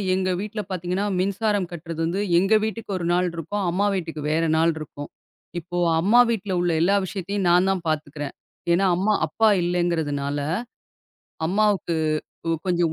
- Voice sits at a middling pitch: Yes, medium, 180 Hz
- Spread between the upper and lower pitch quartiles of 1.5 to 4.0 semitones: Yes, average, 3.1 semitones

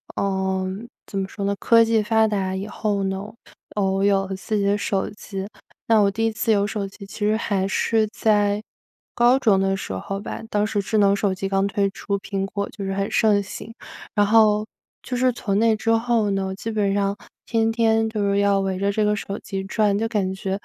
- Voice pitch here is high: Yes, high, 200 Hz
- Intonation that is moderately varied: No, narrow, 1.9 semitones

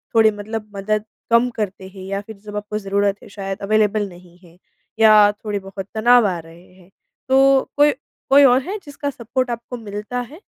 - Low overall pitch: No, high, 210 Hz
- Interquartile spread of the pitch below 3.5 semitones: Yes, average, 3.0 semitones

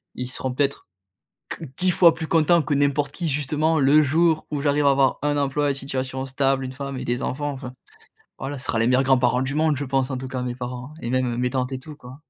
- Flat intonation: Yes, narrow, 2.2 semitones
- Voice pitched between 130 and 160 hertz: Yes, low, 135 Hz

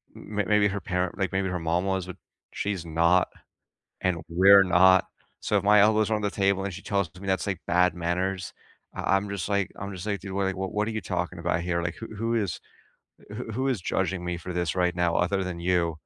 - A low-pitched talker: Yes, very low, 95 Hz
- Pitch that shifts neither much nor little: No, narrow, 2.2 semitones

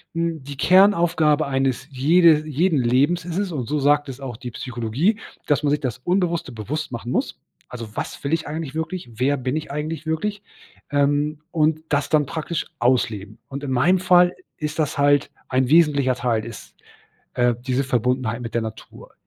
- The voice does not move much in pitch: No, average, 4.0 semitones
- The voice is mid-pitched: Yes, medium, 145 Hz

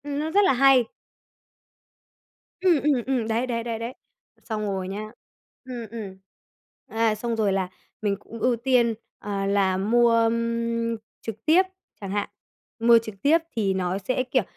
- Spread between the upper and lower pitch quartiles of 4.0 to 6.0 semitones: No, average, 3.3 semitones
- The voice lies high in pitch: Yes, high, 230 Hz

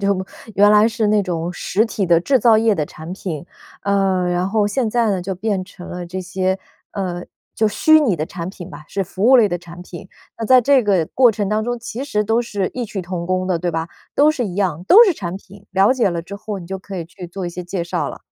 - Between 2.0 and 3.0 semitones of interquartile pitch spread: No, average, 3.5 semitones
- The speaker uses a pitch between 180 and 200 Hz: Yes, high, 195 Hz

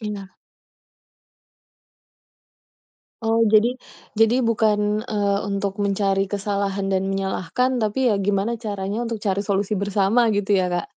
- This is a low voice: No, high, 205 Hz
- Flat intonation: Yes, narrow, 2.0 semitones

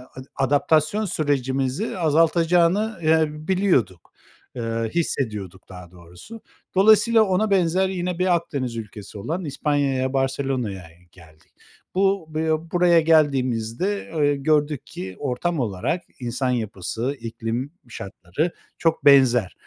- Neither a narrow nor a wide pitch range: No, wide, 6.7 semitones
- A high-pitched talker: No, medium, 145 Hz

